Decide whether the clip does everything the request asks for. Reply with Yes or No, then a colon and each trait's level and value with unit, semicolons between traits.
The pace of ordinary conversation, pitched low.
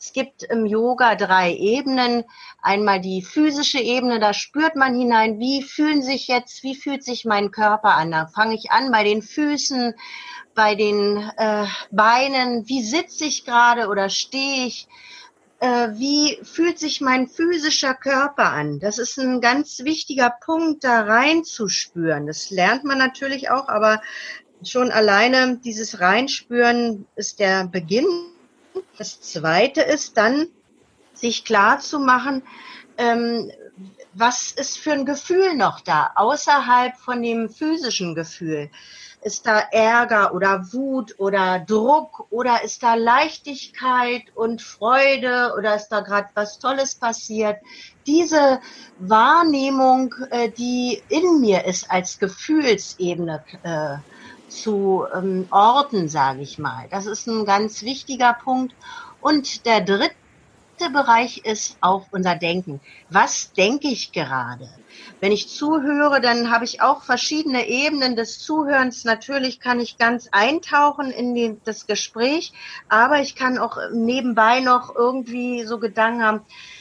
No: average, 135 wpm; high, 240 Hz